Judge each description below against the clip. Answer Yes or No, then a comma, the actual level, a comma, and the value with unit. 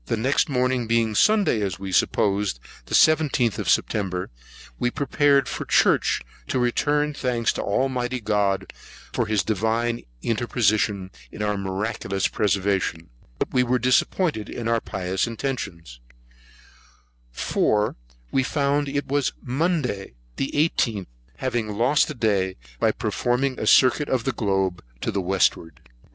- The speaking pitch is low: Yes, low, 115 Hz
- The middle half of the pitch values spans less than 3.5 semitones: No, average, 4.8 semitones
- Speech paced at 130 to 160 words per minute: Yes, slow, 135 wpm